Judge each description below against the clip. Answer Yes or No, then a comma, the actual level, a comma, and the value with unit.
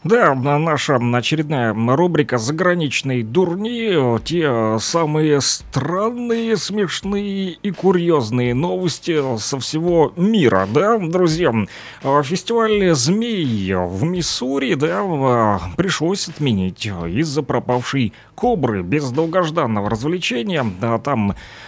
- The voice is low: No, medium, 150 Hz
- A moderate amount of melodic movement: No, wide, 6.5 semitones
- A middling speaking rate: No, slow, 90 wpm